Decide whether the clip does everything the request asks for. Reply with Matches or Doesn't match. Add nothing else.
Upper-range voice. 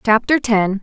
Matches